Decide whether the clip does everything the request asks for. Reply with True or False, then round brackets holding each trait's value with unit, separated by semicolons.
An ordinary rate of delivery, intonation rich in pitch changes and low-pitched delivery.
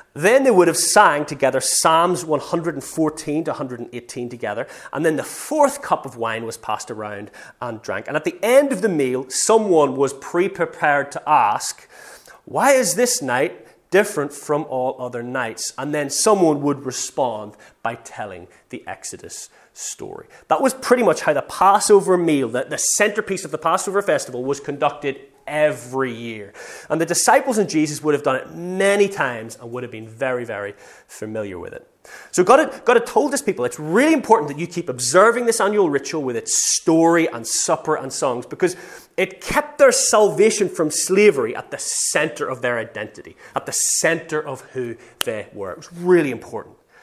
False (180 wpm; 7.0 semitones; 165 Hz)